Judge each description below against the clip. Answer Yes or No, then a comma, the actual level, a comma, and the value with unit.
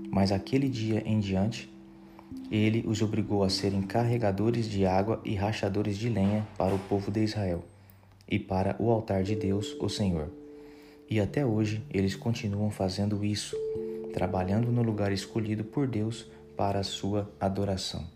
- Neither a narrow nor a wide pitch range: No, narrow, 2.2 semitones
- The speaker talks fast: No, average, 155 wpm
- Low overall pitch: Yes, low, 105 Hz